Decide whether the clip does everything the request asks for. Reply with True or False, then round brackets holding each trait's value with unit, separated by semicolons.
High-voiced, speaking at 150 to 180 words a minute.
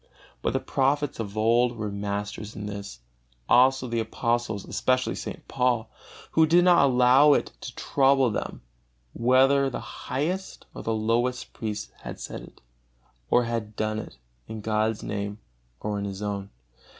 False (115 Hz; 155 wpm)